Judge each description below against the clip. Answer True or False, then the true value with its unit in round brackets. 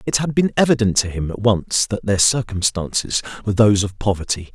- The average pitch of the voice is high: False (105 Hz)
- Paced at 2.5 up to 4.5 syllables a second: False (5.8 syllables/s)